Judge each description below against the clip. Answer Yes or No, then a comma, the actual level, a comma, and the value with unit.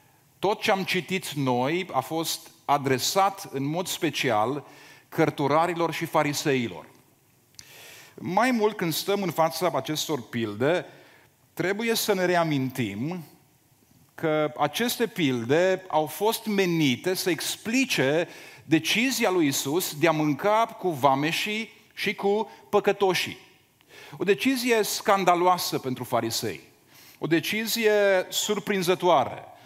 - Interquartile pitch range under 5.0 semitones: No, average, 5.3 semitones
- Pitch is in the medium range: Yes, medium, 170 Hz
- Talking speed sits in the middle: No, slow, 105 wpm